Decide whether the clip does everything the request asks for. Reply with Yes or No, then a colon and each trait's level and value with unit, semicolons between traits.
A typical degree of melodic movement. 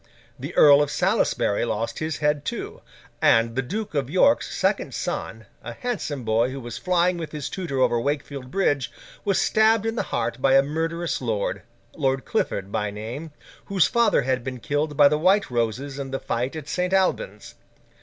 No: wide, 5.9 semitones